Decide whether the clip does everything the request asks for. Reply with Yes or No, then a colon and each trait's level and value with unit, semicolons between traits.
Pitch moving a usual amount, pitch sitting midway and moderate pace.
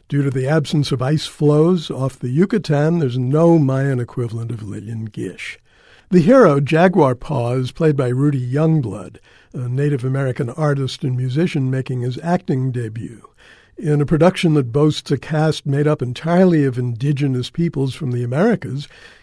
Yes: average, 3.6 semitones; medium, 145 Hz; average, 160 wpm